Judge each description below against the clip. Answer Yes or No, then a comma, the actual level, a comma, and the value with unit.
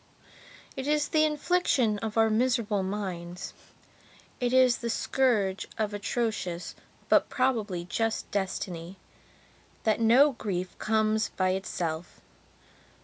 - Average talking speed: No, slow, 105 wpm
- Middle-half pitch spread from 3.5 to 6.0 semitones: Yes, average, 4.5 semitones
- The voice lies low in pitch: No, high, 220 Hz